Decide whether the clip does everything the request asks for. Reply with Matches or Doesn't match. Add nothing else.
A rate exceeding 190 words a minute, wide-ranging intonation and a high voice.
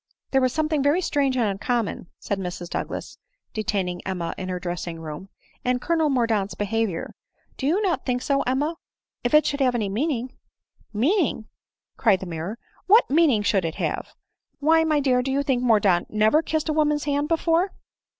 Matches